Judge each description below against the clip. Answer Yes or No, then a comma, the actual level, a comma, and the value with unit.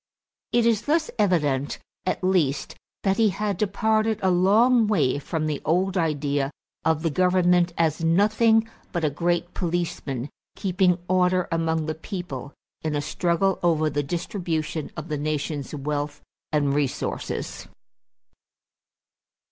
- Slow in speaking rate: Yes, slow, 130 wpm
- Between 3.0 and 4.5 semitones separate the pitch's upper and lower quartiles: Yes, average, 4.2 semitones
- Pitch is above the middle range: No, medium, 170 Hz